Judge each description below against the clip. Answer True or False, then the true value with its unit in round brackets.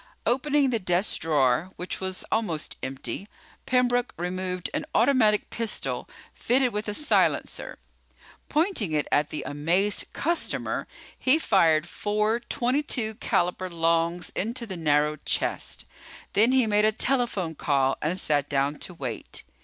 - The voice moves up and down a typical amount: False (6.8 semitones)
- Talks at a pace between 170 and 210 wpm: False (135 wpm)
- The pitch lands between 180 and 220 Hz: True (190 Hz)